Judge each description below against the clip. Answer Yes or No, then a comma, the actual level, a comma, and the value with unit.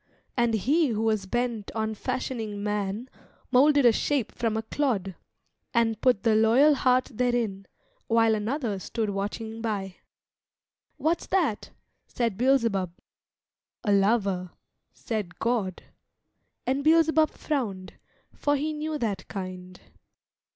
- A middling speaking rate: No, slow, 120 wpm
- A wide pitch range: No, average, 4.2 semitones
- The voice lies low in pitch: No, high, 225 Hz